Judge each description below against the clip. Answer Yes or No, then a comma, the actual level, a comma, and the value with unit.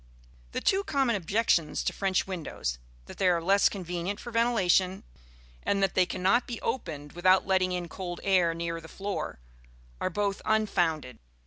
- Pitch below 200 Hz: Yes, medium, 185 Hz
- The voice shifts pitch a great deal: No, average, 2.9 semitones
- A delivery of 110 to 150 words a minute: No, average, 160 wpm